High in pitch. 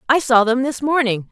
Yes: very high, 250 Hz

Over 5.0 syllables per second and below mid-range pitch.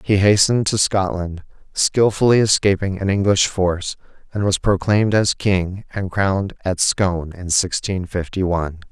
No: 4.8 syllables/s; very low, 95 Hz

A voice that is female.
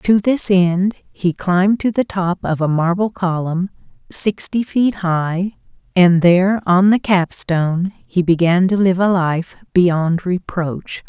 Yes: female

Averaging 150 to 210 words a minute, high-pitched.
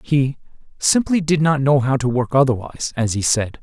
No: average, 200 wpm; low, 135 Hz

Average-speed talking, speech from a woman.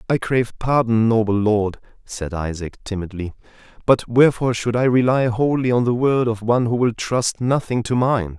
No: average, 180 wpm; male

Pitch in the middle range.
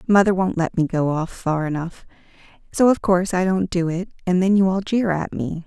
Yes: medium, 180 Hz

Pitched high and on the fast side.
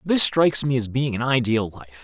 No: low, 130 Hz; fast, 235 wpm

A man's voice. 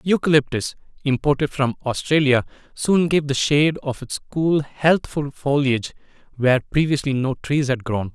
Yes: male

